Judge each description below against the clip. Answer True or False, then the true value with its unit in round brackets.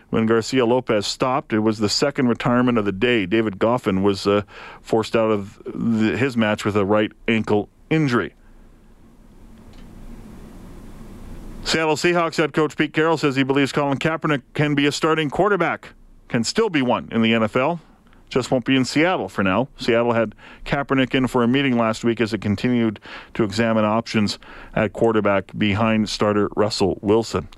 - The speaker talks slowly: False (170 wpm)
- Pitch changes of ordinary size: True (4.3 semitones)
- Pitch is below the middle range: True (115 Hz)